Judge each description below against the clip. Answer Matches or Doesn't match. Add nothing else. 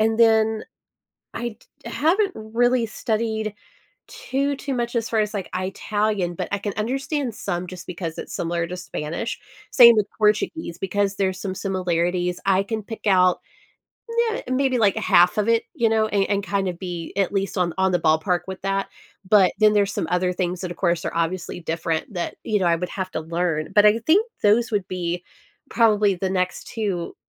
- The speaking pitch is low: Doesn't match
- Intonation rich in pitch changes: Doesn't match